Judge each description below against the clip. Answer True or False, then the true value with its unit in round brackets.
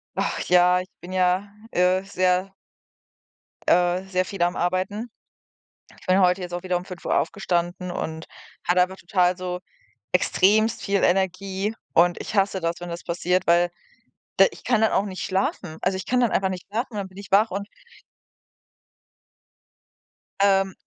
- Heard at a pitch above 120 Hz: True (185 Hz)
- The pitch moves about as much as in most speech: False (1.7 semitones)